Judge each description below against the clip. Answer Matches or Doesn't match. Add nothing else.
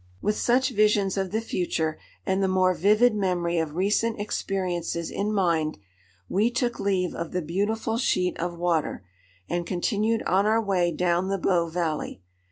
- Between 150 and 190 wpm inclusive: Matches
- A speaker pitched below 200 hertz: Matches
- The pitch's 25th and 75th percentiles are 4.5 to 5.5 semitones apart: Doesn't match